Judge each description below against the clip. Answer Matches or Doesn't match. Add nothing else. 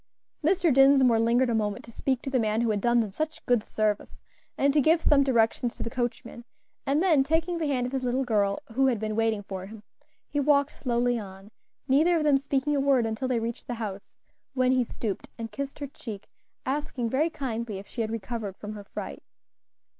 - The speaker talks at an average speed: Doesn't match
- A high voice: Matches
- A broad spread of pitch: Doesn't match